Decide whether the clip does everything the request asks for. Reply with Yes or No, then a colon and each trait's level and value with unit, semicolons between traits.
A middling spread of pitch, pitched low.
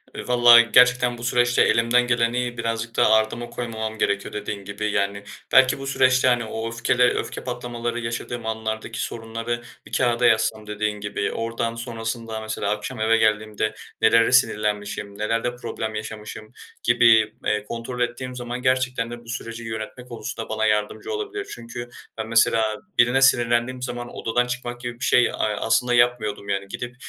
No: narrow, 1.9 semitones; low, 115 Hz